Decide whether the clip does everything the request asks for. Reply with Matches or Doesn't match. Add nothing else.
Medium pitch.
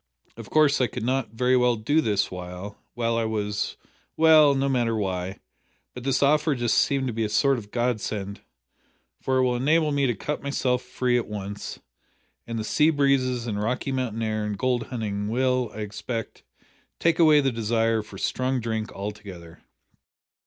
Doesn't match